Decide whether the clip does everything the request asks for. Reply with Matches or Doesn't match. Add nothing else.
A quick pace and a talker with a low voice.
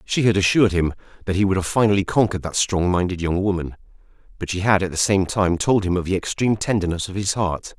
Matches